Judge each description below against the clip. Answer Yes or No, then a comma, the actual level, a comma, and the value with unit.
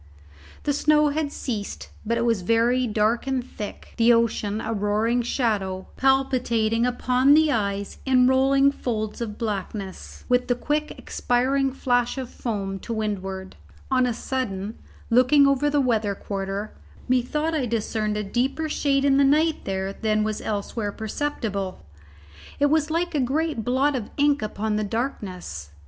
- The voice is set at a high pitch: Yes, high, 240 Hz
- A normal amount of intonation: Yes, average, 4.4 semitones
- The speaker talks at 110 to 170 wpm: Yes, average, 155 wpm